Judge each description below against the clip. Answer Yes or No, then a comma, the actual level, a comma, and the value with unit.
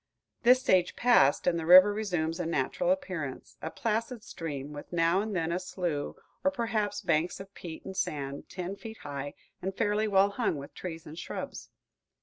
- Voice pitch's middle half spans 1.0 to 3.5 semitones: No, average, 4.8 semitones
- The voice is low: No, medium, 185 Hz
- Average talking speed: Yes, average, 180 wpm